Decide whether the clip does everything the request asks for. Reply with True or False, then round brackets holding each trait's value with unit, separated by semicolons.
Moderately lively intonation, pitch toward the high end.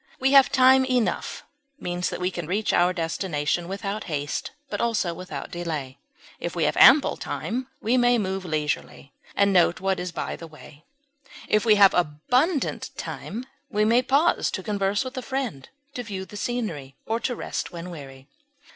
False (6.4 semitones; 195 Hz)